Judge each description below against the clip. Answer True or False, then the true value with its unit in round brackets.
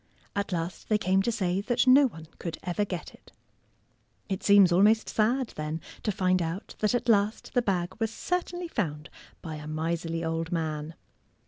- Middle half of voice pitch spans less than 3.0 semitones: False (4.9 semitones)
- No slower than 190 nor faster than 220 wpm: False (180 wpm)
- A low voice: False (185 Hz)